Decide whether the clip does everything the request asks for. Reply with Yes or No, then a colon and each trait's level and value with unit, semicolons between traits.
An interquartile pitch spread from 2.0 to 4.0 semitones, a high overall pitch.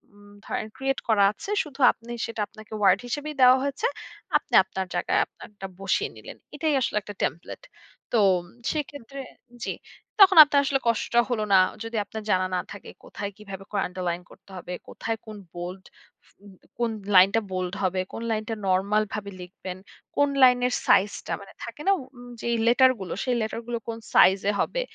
No: average, 4.8 semitones; high, 215 Hz